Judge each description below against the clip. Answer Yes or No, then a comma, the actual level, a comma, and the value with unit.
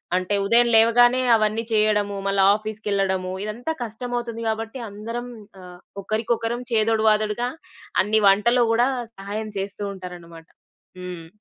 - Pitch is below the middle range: No, high, 215 Hz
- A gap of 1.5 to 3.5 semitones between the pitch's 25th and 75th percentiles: Yes, average, 2.7 semitones